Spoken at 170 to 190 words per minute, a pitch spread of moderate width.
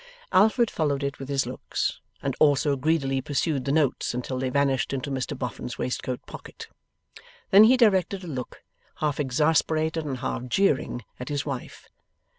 No: average, 160 wpm; average, 3.4 semitones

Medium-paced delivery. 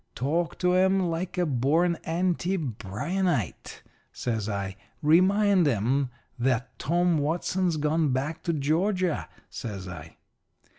No: slow, 115 wpm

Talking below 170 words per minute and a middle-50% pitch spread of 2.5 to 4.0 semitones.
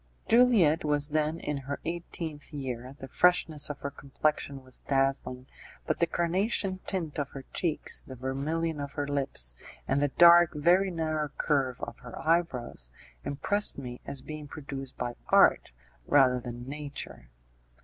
Yes: average, 150 wpm; average, 3.5 semitones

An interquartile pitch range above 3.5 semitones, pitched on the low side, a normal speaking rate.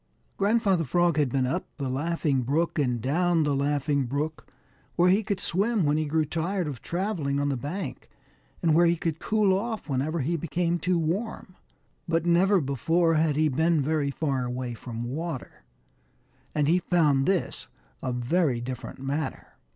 No: average, 4.0 semitones; medium, 155 Hz; average, 170 wpm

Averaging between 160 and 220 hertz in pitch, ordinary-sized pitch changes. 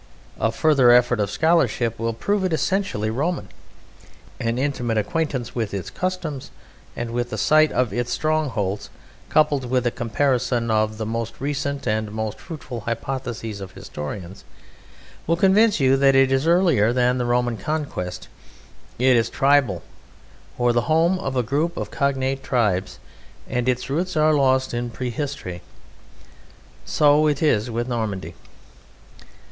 No: low, 125 Hz; average, 4.4 semitones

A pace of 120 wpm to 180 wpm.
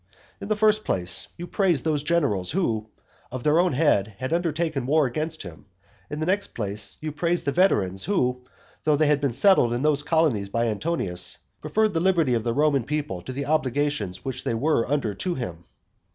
No: average, 195 wpm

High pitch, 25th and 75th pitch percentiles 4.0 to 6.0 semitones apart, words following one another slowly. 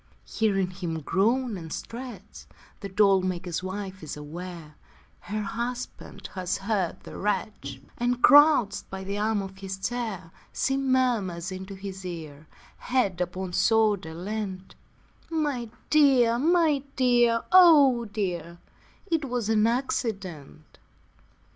Yes: high, 205 Hz; average, 4.8 semitones; slow, 120 wpm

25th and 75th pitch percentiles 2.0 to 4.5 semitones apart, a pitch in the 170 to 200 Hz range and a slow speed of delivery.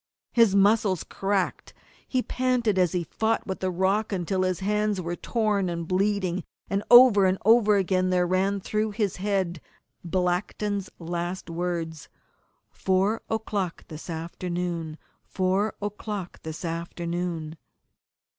Yes: average, 2.9 semitones; medium, 185 Hz; slow, 125 wpm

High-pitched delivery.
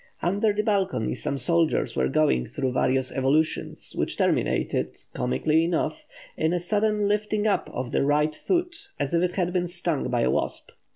No: medium, 170 Hz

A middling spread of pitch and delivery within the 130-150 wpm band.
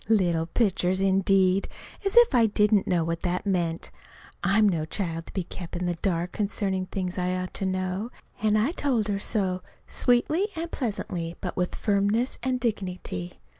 No: average, 3.2 semitones; average, 170 wpm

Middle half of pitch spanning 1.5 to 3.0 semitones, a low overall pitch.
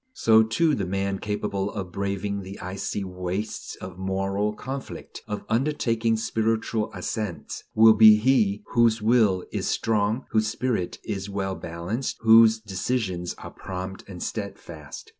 Yes: average, 2.7 semitones; low, 105 Hz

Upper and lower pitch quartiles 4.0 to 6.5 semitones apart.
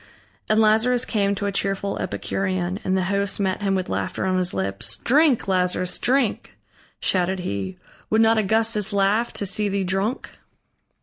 No: average, 2.7 semitones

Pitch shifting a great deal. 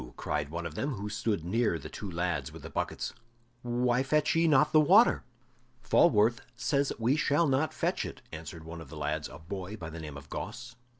Yes: wide, 8.3 semitones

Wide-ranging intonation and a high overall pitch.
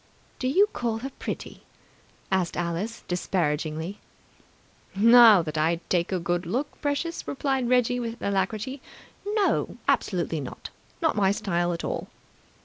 Yes: wide, 6.2 semitones; high, 205 Hz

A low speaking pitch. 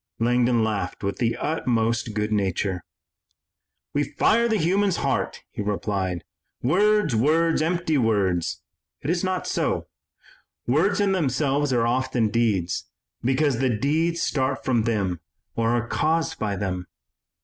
Yes: low, 125 Hz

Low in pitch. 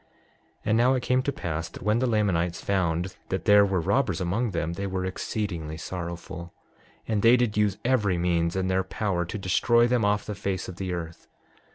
Yes: very low, 95 Hz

